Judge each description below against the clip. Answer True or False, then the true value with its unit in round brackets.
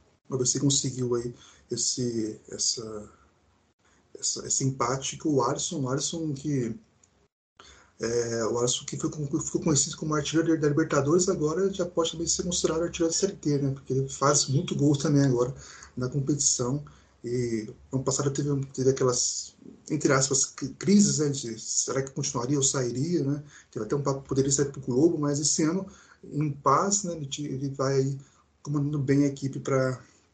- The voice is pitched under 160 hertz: True (140 Hz)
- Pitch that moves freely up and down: False (2.7 semitones)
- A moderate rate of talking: True (170 wpm)